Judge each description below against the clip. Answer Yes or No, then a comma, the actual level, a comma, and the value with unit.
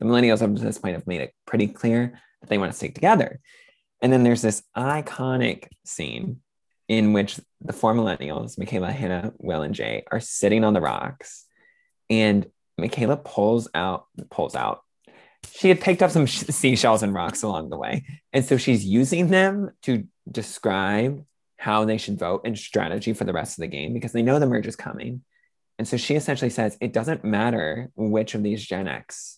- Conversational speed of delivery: Yes, average, 190 wpm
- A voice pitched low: Yes, low, 120 Hz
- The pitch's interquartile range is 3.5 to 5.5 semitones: Yes, average, 4.3 semitones